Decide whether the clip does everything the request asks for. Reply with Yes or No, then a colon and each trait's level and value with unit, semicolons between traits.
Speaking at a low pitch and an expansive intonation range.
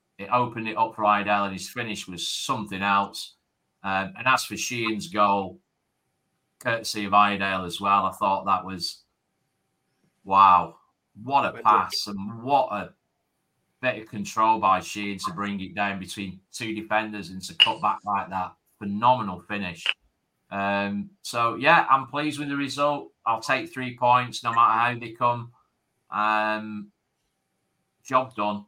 No: low, 105 Hz; average, 3.2 semitones